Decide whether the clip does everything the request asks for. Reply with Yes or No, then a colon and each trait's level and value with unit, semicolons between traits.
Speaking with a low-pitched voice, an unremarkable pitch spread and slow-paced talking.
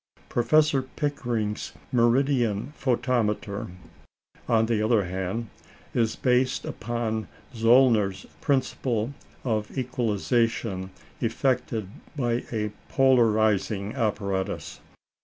Yes: low, 115 Hz; average, 3.0 semitones; slow, 80 wpm